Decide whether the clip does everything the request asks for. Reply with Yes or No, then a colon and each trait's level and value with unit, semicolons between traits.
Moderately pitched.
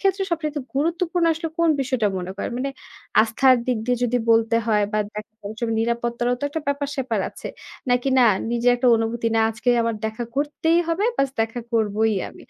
No: high, 245 Hz